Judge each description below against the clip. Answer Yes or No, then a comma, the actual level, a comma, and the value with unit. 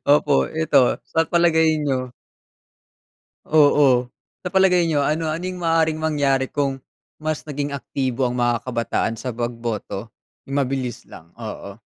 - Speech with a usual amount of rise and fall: Yes, average, 4.2 semitones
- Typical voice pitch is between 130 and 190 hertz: Yes, medium, 140 Hz